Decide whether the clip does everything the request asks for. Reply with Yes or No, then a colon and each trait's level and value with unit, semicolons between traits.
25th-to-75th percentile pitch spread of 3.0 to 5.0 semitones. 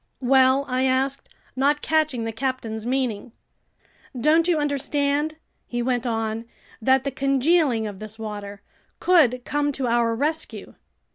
Yes: average, 3.9 semitones